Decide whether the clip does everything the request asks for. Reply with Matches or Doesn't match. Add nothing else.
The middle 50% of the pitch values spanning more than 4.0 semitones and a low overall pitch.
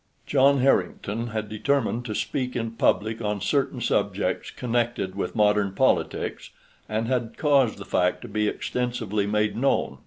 Doesn't match